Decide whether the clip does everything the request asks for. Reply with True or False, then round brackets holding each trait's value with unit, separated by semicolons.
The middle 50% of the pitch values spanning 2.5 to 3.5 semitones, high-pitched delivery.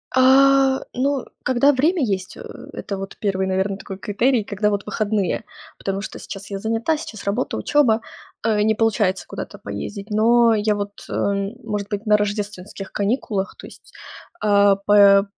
True (2.9 semitones; 210 Hz)